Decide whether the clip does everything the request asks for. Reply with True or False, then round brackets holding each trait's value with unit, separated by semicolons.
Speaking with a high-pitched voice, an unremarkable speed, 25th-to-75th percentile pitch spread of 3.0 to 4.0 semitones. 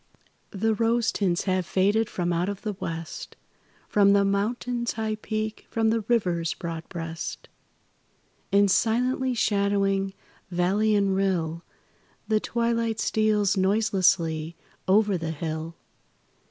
False (200 Hz; 120 wpm; 3.7 semitones)